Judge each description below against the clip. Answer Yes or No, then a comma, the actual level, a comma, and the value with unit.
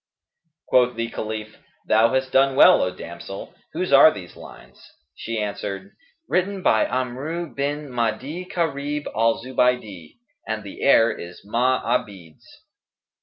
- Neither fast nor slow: No, slow, 125 wpm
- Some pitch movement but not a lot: Yes, average, 4.4 semitones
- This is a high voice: No, low, 120 Hz